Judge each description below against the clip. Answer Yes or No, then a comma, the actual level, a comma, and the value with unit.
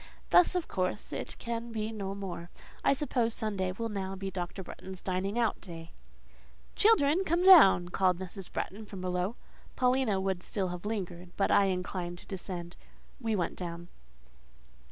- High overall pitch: Yes, high, 195 Hz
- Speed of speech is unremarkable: Yes, average, 165 wpm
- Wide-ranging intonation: No, average, 3.9 semitones